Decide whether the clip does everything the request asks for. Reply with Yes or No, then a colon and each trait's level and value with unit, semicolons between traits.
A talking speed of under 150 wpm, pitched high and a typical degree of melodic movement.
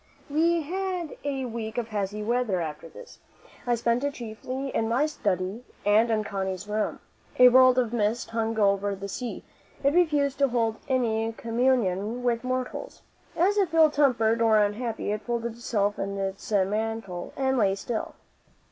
No: average, 165 wpm; high, 230 Hz; average, 3.8 semitones